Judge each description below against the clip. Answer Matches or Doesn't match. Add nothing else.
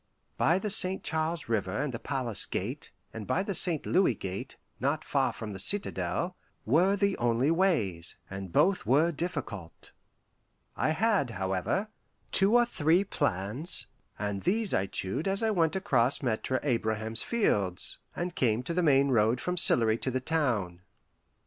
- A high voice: Doesn't match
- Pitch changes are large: Matches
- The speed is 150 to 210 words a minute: Matches